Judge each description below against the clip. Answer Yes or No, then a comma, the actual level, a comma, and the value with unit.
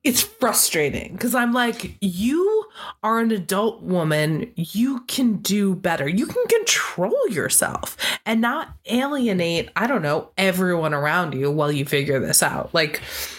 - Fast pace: No, average, 150 wpm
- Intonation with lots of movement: Yes, wide, 6.4 semitones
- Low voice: No, high, 205 Hz